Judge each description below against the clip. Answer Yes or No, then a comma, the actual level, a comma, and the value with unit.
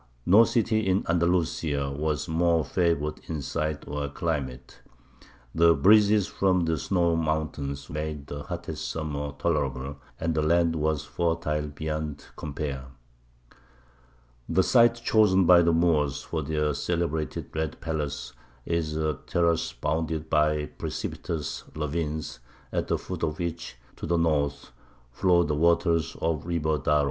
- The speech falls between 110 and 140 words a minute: Yes, slow, 135 wpm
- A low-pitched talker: Yes, very low, 80 Hz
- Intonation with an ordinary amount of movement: No, narrow, 2.3 semitones